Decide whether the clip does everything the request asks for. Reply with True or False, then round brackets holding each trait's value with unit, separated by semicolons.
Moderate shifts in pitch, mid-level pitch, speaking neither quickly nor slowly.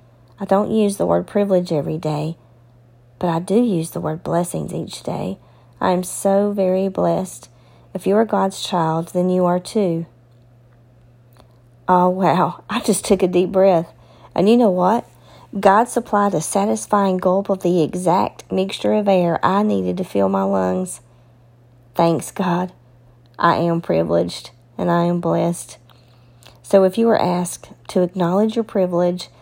False (8.0 semitones; 175 Hz; 160 wpm)